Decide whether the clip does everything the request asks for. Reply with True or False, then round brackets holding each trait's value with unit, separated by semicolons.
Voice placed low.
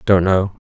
True (95 Hz)